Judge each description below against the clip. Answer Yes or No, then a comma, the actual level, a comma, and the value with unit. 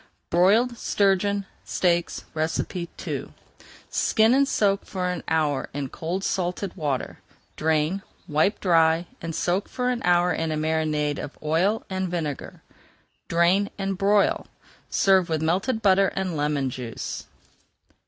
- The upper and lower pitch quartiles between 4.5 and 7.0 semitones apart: No, average, 3.7 semitones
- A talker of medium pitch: Yes, medium, 175 Hz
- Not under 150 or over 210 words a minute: No, slow, 135 wpm